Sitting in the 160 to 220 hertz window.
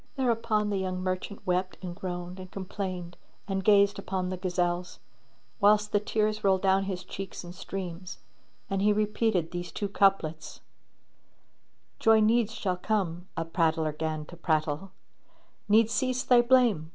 Yes: high, 190 Hz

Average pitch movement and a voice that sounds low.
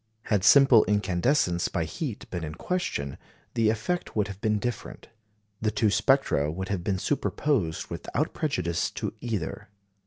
No: wide, 5.7 semitones; low, 105 Hz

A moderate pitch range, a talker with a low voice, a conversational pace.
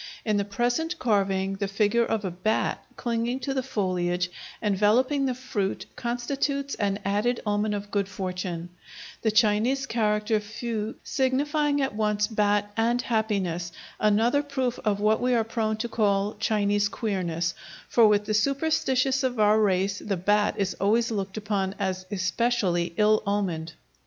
No: average, 3.2 semitones; high, 210 Hz; average, 150 wpm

